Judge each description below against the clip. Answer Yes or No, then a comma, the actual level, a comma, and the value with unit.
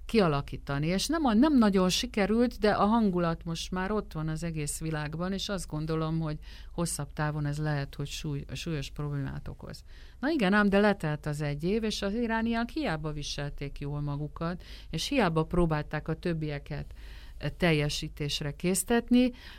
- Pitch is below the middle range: No, medium, 160 Hz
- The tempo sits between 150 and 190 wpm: Yes, fast, 155 wpm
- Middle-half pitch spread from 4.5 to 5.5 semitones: Yes, average, 5.2 semitones